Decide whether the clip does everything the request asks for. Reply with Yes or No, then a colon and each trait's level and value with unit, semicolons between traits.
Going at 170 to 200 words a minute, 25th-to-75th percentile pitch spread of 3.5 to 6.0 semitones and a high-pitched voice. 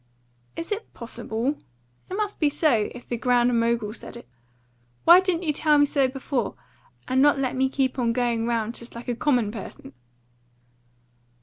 Yes: average, 175 wpm; average, 3.8 semitones; very high, 255 Hz